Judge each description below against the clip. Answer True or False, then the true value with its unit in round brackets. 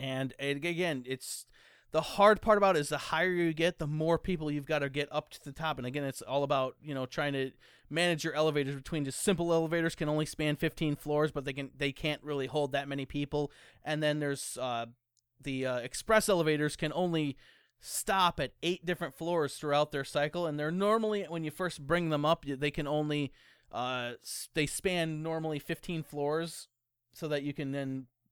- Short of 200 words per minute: False (205 wpm)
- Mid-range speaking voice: True (150 Hz)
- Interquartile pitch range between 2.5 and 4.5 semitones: True (2.9 semitones)